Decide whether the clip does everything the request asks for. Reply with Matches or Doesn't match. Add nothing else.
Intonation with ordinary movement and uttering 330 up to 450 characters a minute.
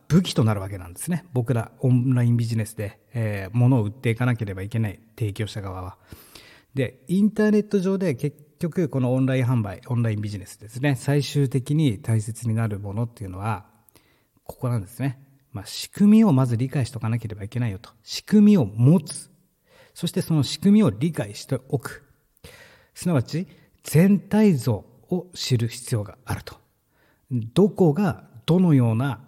Doesn't match